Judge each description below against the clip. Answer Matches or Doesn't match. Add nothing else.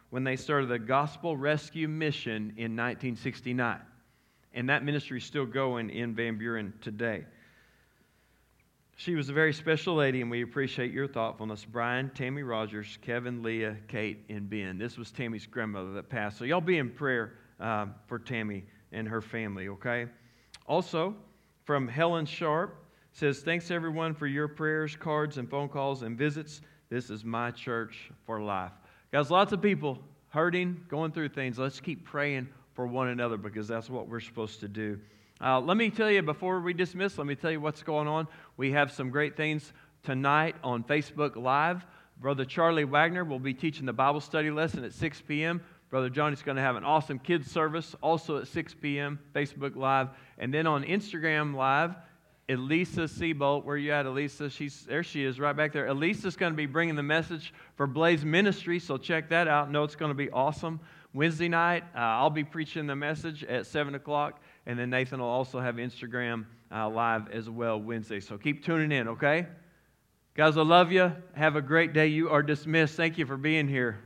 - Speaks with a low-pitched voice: Doesn't match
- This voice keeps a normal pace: Matches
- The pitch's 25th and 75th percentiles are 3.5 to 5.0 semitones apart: Matches